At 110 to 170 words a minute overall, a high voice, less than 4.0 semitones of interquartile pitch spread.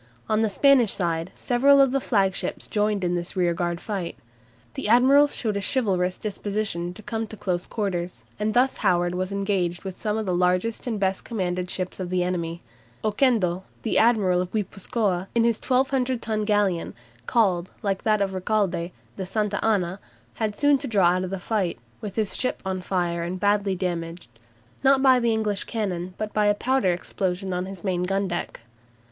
No: average, 185 wpm; high, 195 Hz; average, 3.4 semitones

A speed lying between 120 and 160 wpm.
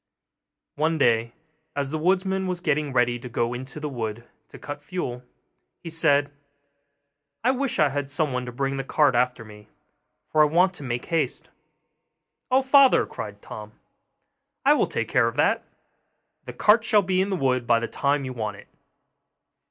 No: average, 175 wpm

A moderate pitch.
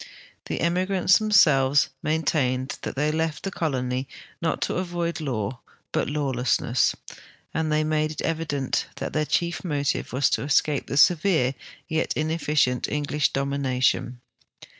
Yes: medium, 150 Hz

